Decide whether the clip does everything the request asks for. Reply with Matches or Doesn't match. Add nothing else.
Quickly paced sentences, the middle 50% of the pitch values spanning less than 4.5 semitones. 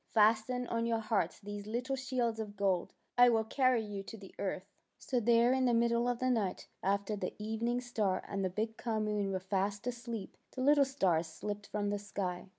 Matches